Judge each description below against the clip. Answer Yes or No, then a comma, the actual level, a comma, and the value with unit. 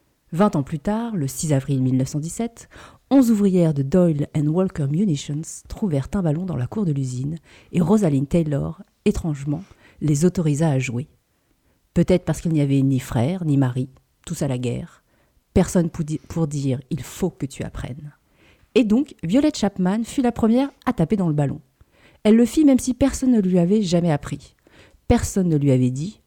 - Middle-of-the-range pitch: Yes, medium, 165 Hz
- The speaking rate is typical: Yes, average, 185 wpm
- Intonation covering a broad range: Yes, wide, 6.3 semitones